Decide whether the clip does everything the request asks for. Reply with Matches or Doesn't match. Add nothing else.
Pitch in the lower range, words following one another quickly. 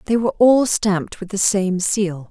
Doesn't match